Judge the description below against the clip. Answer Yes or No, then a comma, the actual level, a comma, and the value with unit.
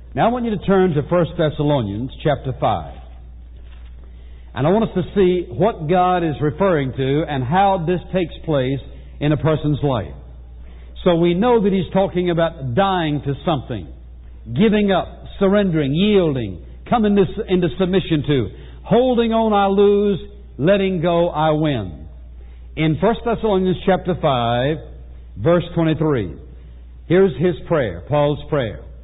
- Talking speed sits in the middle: Yes, average, 145 wpm